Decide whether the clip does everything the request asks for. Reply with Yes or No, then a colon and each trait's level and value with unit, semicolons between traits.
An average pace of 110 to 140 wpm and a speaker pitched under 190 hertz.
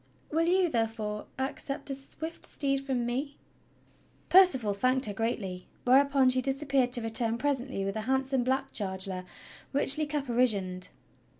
No: slow, 135 wpm; very high, 255 Hz